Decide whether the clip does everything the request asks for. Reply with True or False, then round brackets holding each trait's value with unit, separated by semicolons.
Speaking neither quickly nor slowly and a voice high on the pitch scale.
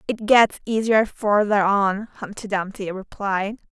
False (130 wpm; 205 Hz)